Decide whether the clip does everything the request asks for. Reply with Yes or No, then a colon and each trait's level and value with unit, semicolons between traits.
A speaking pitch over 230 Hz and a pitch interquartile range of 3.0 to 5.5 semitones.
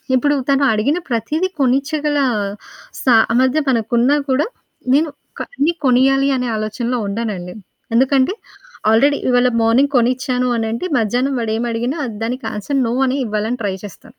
Yes: very high, 250 Hz; average, 3.4 semitones